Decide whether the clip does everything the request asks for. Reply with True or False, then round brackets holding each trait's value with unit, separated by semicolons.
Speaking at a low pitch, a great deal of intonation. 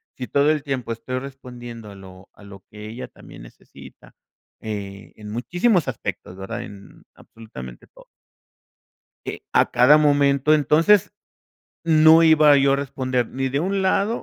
True (130 Hz; 6.0 semitones)